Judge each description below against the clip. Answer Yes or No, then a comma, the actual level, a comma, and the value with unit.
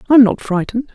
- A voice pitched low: No, high, 235 Hz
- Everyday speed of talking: Yes, average, 190 wpm